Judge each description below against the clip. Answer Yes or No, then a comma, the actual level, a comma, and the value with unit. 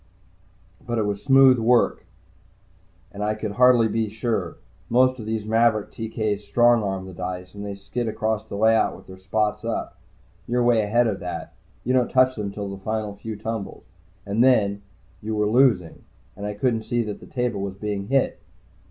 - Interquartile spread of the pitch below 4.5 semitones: Yes, average, 2.7 semitones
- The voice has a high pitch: No, low, 110 Hz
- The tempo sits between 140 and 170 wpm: No, average, 185 wpm